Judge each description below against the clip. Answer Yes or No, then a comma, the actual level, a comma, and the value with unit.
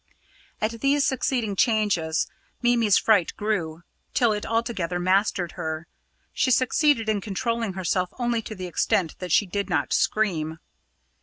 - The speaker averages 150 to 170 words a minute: No, average, 140 wpm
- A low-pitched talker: No, high, 205 Hz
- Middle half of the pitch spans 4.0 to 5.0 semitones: Yes, average, 4.5 semitones